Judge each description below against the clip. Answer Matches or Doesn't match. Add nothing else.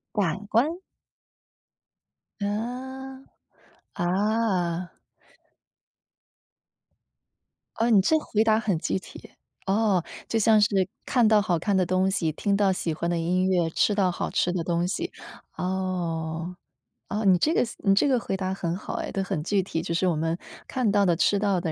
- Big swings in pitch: Doesn't match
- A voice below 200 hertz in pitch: Matches